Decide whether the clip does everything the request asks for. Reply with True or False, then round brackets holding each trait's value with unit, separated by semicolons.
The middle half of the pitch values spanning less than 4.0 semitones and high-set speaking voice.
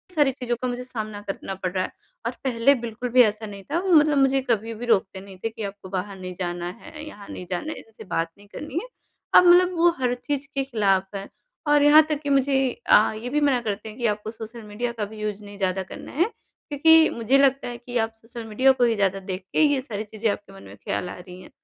False (5.1 semitones; 225 Hz)